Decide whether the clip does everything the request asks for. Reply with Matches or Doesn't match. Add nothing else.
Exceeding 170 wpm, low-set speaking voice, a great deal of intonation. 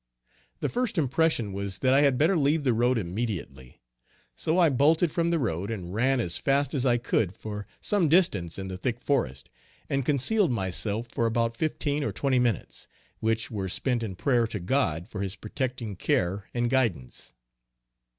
Matches